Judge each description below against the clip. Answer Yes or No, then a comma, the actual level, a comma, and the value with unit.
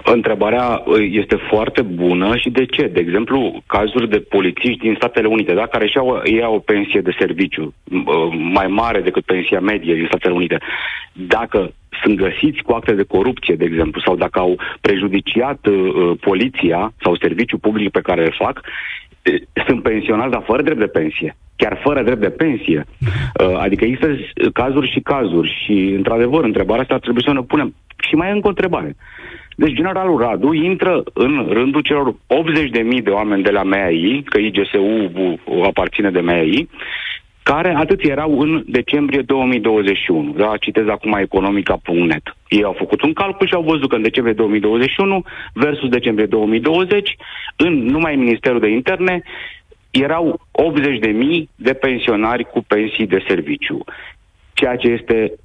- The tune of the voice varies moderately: No, wide, 6.8 semitones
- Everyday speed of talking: Yes, average, 160 wpm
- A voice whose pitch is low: Yes, low, 115 Hz